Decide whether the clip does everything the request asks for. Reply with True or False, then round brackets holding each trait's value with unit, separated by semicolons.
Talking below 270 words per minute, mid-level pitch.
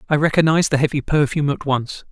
True (200 wpm; 145 Hz)